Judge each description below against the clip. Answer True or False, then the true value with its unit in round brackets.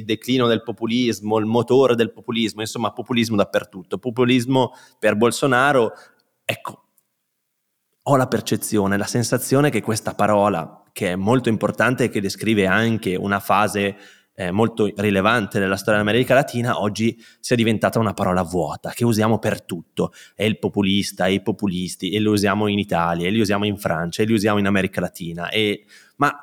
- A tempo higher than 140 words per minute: True (165 wpm)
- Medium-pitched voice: False (105 Hz)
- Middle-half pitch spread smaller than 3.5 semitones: True (2.5 semitones)